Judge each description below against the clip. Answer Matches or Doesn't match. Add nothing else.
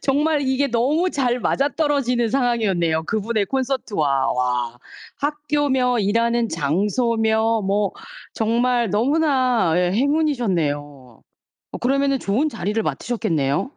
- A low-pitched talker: Doesn't match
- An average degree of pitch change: Doesn't match